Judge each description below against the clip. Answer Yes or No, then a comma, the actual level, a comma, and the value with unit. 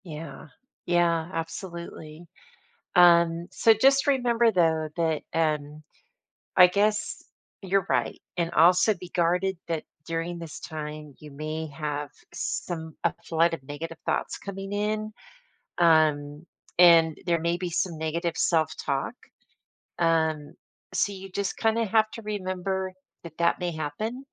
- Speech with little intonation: No, average, 3.1 semitones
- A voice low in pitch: No, medium, 170 Hz